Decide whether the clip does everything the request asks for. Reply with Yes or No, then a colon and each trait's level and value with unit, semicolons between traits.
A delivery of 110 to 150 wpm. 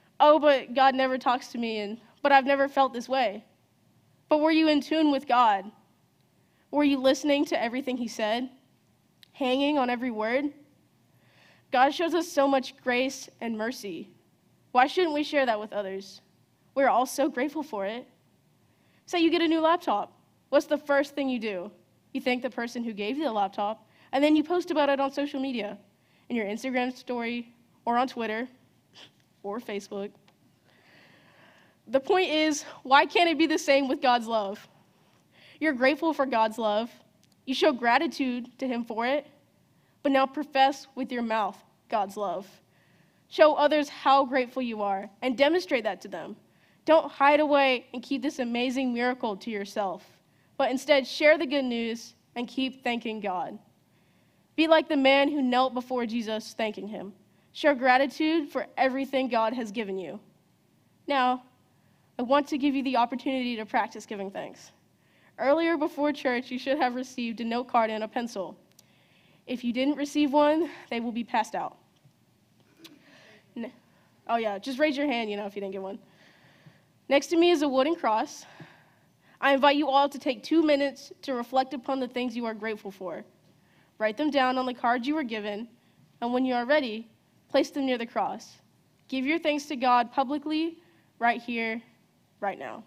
No: average, 180 wpm